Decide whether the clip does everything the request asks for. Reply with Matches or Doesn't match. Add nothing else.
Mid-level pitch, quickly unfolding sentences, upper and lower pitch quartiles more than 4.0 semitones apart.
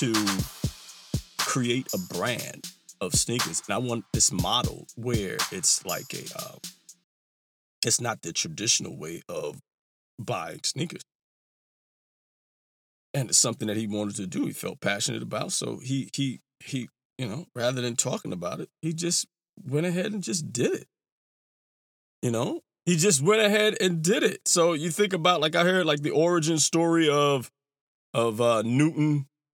Doesn't match